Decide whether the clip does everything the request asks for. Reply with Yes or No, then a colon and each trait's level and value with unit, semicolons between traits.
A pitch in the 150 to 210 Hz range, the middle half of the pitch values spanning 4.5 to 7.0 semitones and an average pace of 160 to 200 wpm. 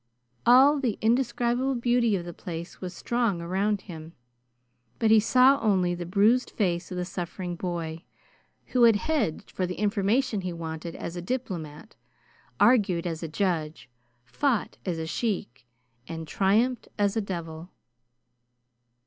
No: high, 190 Hz; wide, 5.6 semitones; average, 145 wpm